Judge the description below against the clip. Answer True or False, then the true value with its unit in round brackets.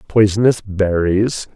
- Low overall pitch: True (100 Hz)